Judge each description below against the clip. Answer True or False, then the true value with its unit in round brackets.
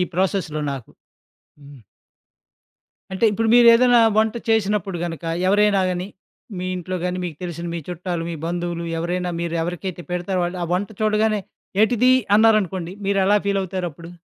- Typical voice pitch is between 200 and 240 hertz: False (185 Hz)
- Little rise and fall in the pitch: False (3.3 semitones)